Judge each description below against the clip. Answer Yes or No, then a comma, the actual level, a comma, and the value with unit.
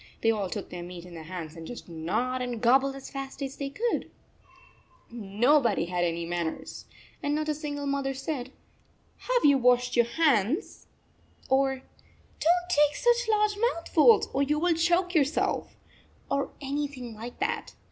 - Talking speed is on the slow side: No, average, 170 wpm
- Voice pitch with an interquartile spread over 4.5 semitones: Yes, wide, 5.5 semitones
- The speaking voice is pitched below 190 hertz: No, very high, 270 Hz